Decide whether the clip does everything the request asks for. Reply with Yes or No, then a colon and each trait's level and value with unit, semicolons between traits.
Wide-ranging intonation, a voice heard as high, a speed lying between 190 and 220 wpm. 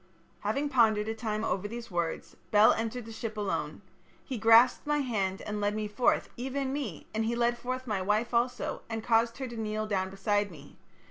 No: narrow, 2.5 semitones; high, 225 Hz; average, 200 wpm